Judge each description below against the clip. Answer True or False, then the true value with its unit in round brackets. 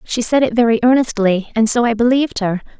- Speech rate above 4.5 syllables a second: True (6.0 syllables/s)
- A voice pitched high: True (230 Hz)